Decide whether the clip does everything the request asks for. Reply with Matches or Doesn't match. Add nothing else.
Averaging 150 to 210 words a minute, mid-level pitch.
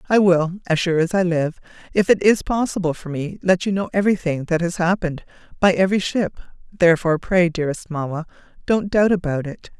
Matches